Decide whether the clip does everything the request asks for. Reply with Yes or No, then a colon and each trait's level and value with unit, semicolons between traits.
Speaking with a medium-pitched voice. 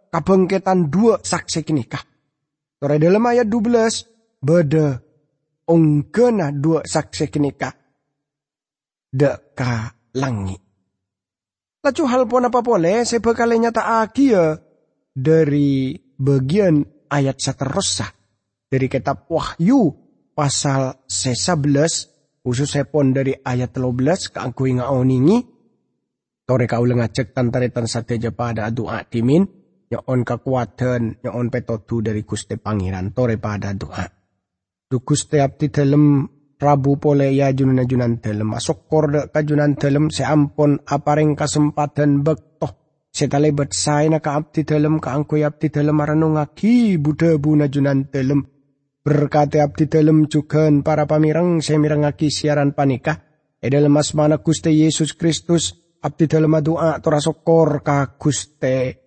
Yes: medium, 145 Hz